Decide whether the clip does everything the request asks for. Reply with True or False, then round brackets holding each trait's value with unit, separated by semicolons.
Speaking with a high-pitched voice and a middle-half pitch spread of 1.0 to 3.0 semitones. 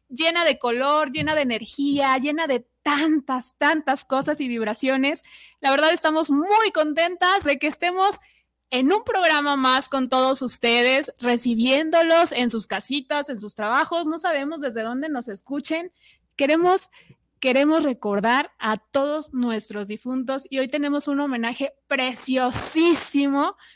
False (280 Hz; 3.6 semitones)